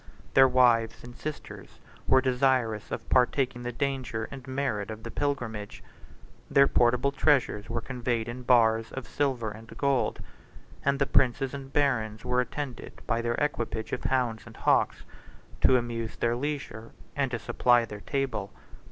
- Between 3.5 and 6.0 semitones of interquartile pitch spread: No, average, 2.8 semitones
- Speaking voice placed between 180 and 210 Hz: No, low, 125 Hz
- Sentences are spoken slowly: No, average, 155 wpm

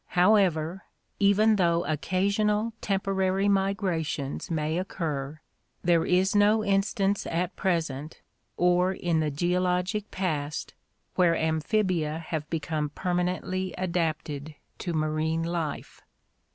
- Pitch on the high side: No, medium, 175 Hz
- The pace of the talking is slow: Yes, slow, 105 wpm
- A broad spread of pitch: No, average, 3.4 semitones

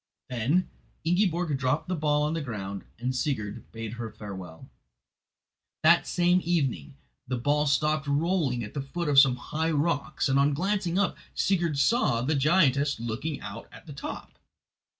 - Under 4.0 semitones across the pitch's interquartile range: No, average, 5.1 semitones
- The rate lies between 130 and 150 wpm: No, average, 160 wpm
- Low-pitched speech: No, medium, 145 Hz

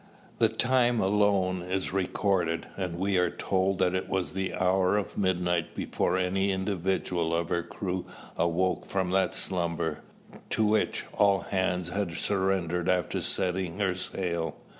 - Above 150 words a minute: No, average, 145 wpm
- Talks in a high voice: No, very low, 95 Hz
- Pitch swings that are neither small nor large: No, narrow, 1.6 semitones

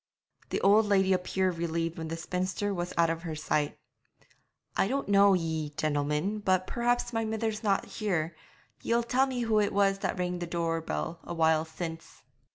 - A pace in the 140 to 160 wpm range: No, average, 185 wpm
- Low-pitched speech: No, medium, 180 Hz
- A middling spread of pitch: Yes, average, 4.1 semitones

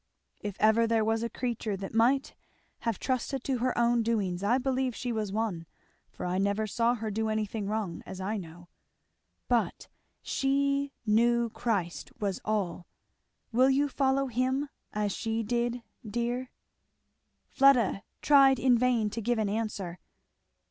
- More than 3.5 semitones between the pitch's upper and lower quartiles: No, average, 3.2 semitones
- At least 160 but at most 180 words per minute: No, average, 150 wpm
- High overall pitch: Yes, high, 230 Hz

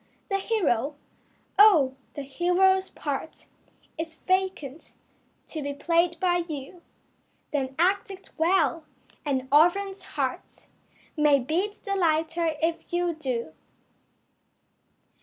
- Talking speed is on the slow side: Yes, slow, 105 wpm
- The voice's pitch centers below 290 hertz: No, very high, 330 Hz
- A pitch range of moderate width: Yes, average, 4.5 semitones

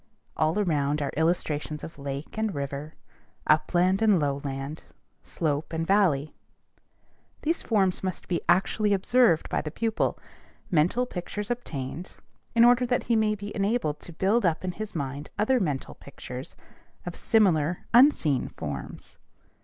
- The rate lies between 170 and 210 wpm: No, average, 140 wpm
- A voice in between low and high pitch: Yes, medium, 175 Hz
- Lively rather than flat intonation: Yes, wide, 6.0 semitones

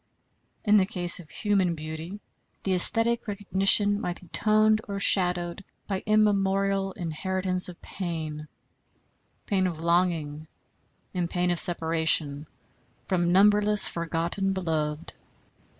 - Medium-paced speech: No, slow, 115 wpm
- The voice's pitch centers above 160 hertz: Yes, medium, 185 Hz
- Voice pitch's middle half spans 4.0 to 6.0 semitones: No, average, 3.1 semitones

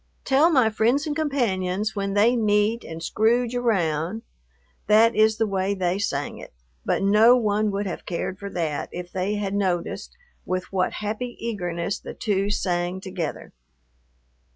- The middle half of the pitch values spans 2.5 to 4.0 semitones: Yes, average, 3.4 semitones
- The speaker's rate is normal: Yes, average, 155 wpm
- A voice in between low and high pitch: No, high, 205 Hz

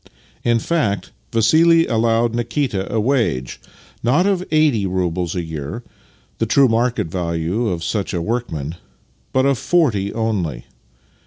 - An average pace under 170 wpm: Yes, average, 145 wpm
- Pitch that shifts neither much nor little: No, wide, 6.0 semitones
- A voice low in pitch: Yes, low, 115 Hz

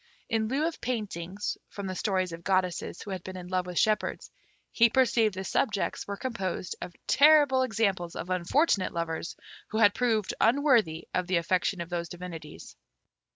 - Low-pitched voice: No, high, 195 Hz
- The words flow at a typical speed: Yes, average, 170 wpm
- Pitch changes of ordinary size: Yes, average, 4.3 semitones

